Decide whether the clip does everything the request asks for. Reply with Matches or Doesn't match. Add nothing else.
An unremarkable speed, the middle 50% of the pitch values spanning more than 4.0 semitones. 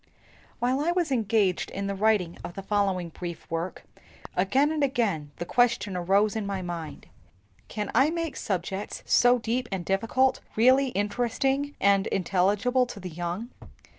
Matches